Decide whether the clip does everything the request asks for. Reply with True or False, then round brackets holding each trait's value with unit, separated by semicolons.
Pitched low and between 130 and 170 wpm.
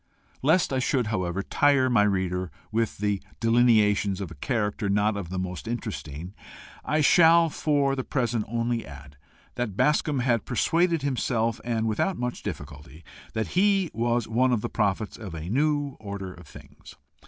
True (115 Hz; 165 wpm)